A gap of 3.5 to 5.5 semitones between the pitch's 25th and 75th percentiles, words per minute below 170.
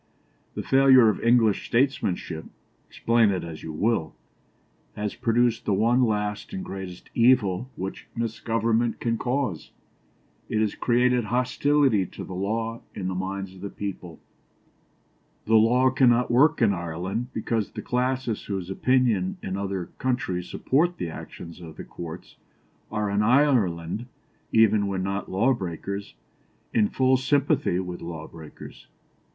Yes: average, 4.7 semitones; average, 140 wpm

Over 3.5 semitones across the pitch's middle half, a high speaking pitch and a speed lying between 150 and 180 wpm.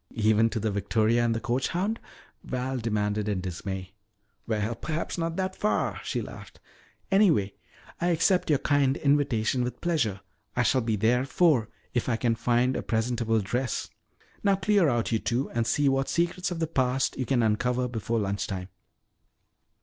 No: average, 4.8 semitones; low, 120 Hz; average, 175 wpm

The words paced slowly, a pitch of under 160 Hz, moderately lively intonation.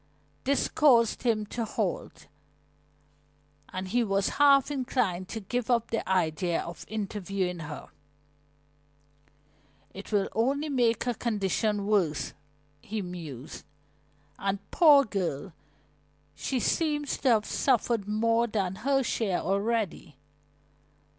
No: slow, 115 wpm; high, 215 Hz; average, 4.4 semitones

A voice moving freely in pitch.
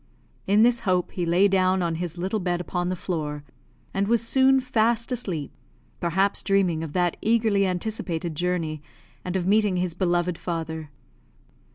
No: average, 3.2 semitones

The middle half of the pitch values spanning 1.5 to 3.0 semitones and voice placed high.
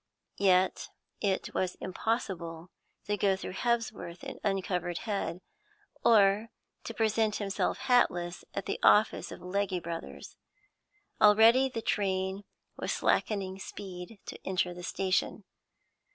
Yes: average, 2.7 semitones; high, 195 Hz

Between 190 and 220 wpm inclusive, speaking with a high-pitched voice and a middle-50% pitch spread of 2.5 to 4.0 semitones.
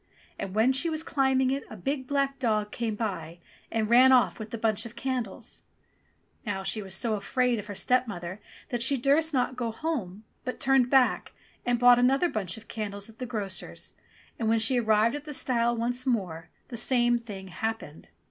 Yes: average, 195 wpm; high, 235 Hz; average, 3.4 semitones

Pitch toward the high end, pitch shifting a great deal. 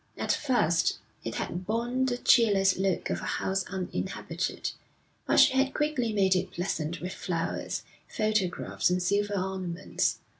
No: high, 195 Hz; average, 4.1 semitones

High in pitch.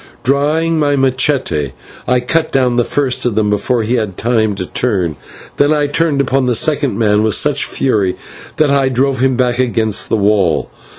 No: low, 125 Hz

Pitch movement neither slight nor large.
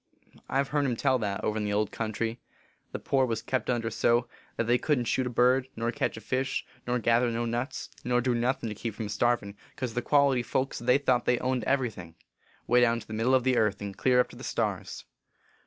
No: narrow, 2.2 semitones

